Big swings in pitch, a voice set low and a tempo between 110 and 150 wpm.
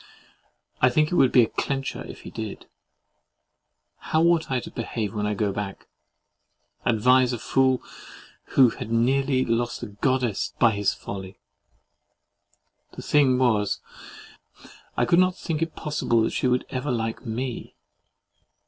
No: average, 3.3 semitones; low, 125 Hz; average, 145 wpm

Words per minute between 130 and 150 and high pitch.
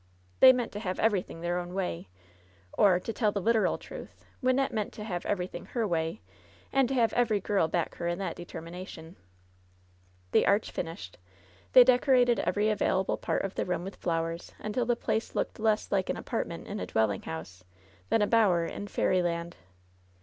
No: average, 185 wpm; high, 195 Hz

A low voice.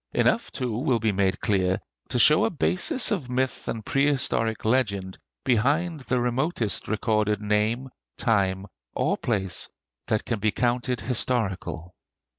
Yes: low, 115 Hz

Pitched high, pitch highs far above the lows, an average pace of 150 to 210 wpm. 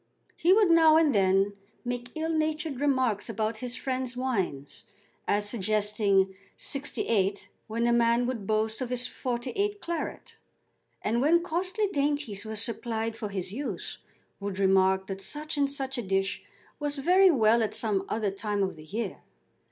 Yes: high, 235 Hz; wide, 5.9 semitones; average, 160 wpm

